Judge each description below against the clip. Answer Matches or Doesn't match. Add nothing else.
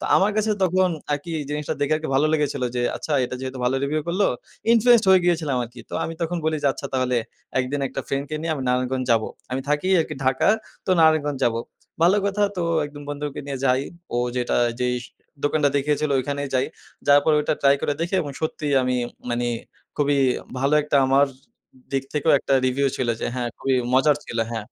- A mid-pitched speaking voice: Matches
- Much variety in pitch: Doesn't match